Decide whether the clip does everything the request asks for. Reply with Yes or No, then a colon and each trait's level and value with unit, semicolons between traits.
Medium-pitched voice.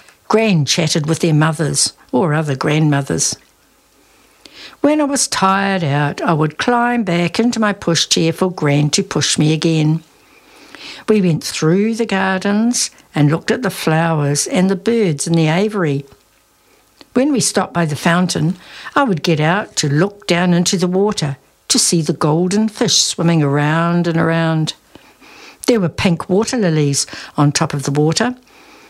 Yes: medium, 175 Hz